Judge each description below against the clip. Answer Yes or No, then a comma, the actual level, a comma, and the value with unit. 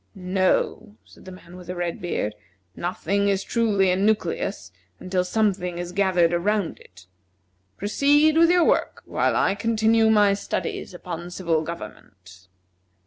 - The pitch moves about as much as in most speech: Yes, average, 3.5 semitones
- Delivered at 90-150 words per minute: Yes, average, 140 wpm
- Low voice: No, medium, 185 Hz